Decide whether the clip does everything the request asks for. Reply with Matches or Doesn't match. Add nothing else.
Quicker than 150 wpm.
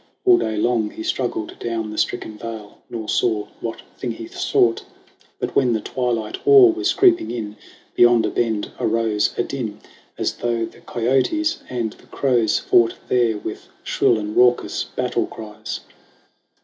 Matches